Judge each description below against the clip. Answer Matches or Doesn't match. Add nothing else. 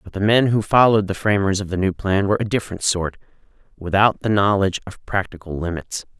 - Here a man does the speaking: Matches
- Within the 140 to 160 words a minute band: Doesn't match